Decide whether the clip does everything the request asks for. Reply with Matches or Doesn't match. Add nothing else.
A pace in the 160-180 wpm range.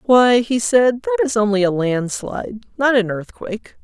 Matches